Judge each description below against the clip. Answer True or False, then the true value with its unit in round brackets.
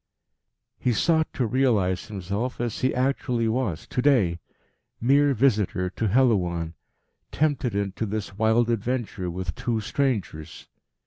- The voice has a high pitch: False (115 Hz)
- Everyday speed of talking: False (125 wpm)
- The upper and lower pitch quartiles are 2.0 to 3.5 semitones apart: False (5.1 semitones)